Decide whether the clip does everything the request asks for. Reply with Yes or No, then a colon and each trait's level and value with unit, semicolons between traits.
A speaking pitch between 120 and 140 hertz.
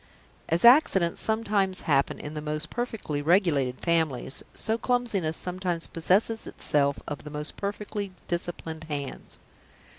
No: medium, 170 Hz